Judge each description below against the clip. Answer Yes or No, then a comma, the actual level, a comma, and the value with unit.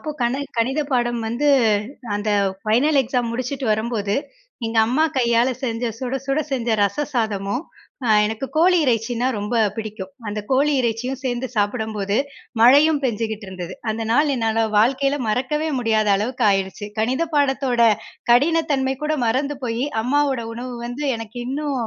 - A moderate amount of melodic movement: Yes, average, 3.5 semitones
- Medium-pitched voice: No, high, 245 Hz